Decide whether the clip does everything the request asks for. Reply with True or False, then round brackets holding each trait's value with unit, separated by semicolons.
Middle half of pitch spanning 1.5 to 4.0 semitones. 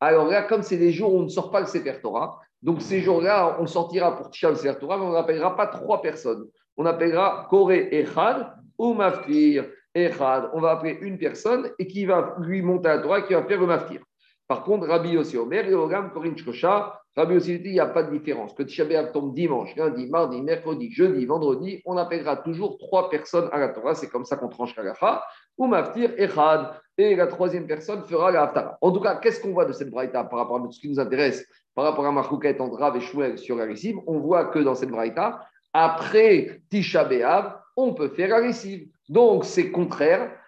False (4.9 semitones)